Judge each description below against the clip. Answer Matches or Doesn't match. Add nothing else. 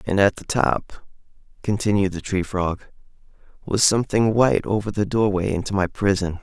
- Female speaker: Doesn't match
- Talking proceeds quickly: Doesn't match